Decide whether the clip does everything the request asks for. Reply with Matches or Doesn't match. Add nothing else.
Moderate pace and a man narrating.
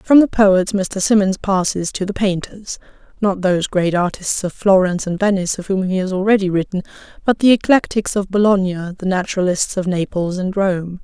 Doesn't match